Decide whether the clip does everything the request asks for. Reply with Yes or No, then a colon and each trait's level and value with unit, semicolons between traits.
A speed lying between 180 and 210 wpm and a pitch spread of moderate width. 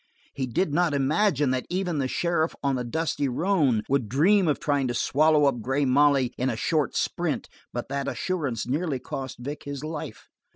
Yes: average, 190 wpm; average, 3.4 semitones